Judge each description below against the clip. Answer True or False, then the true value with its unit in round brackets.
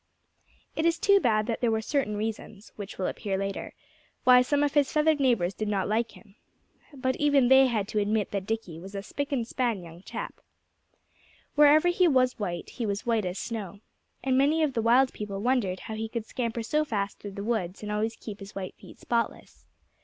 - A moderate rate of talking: False (210 wpm)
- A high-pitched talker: True (225 Hz)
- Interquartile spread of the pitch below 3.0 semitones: False (4.6 semitones)